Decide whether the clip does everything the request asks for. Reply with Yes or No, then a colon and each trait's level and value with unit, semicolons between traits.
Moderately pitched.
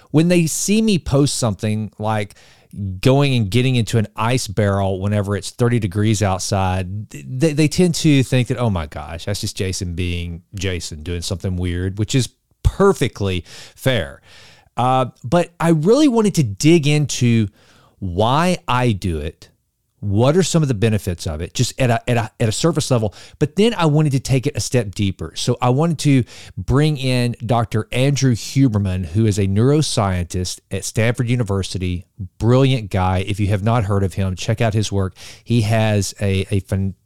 No: low, 110 Hz